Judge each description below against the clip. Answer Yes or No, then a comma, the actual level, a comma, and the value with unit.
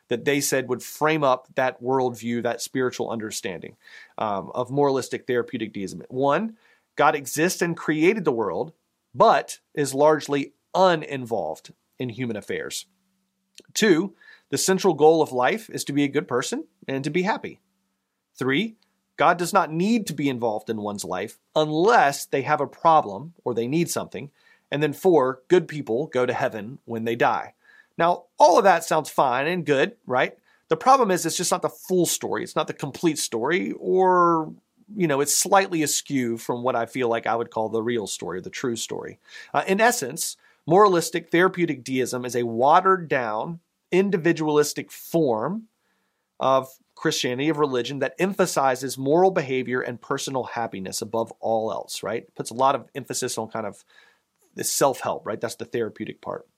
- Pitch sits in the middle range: Yes, medium, 145 Hz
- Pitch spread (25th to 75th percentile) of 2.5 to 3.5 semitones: No, wide, 5.5 semitones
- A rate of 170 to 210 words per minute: Yes, average, 175 wpm